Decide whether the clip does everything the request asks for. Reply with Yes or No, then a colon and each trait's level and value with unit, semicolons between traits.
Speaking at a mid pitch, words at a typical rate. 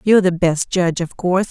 No: medium, 180 Hz; fast, 240 wpm